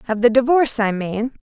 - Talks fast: Yes, fast, 210 wpm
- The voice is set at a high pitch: Yes, high, 235 Hz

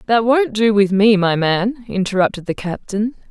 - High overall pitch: Yes, high, 210 Hz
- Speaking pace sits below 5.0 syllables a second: Yes, 4.7 syllables/s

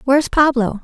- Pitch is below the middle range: No, very high, 265 Hz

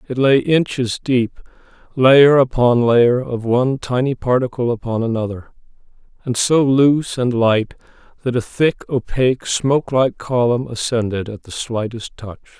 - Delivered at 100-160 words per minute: Yes, average, 145 wpm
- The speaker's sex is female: No, male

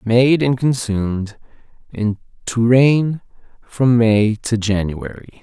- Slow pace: Yes, slow, 100 wpm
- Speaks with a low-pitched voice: Yes, low, 115 Hz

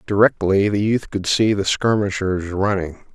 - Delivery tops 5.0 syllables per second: No, 4.5 syllables/s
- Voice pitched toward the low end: Yes, low, 100 Hz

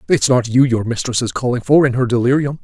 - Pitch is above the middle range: No, low, 125 Hz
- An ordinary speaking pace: No, fast, 250 wpm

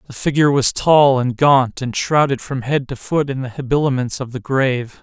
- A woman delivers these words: No, male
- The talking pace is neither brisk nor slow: No, fast, 215 wpm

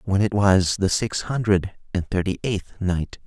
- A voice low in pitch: Yes, very low, 95 Hz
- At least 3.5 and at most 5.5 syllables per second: Yes, 4.4 syllables/s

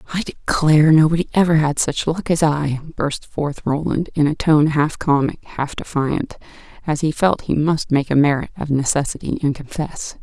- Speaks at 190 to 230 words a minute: No, average, 180 wpm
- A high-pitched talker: No, medium, 155 Hz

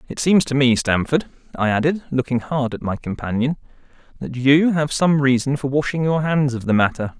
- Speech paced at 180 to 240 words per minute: Yes, average, 200 wpm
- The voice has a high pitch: No, medium, 140 Hz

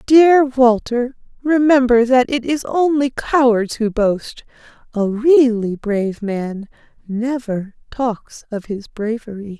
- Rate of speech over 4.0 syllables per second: No, 3.6 syllables/s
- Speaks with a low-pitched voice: No, high, 240 Hz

